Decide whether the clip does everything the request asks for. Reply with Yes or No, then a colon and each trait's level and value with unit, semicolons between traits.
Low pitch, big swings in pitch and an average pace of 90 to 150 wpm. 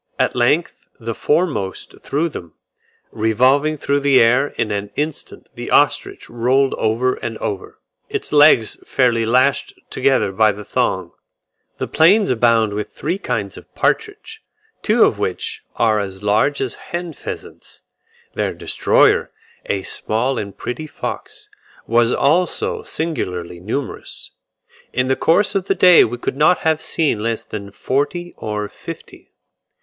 Yes: low, 125 Hz; wide, 5.8 semitones; average, 145 wpm